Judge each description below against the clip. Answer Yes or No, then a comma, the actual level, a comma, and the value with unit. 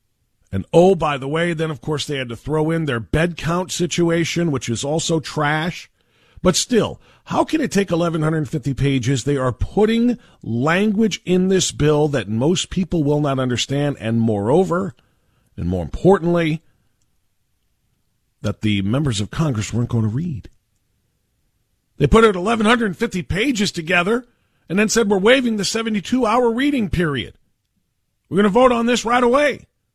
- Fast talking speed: No, average, 160 wpm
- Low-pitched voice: No, medium, 155 Hz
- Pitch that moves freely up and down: Yes, wide, 8.2 semitones